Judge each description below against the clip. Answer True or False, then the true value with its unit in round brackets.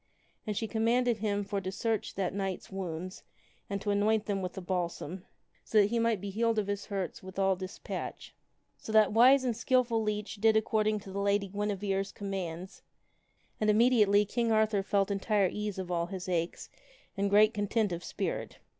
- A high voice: True (205 Hz)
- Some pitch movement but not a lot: False (2.2 semitones)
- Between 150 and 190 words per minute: True (185 wpm)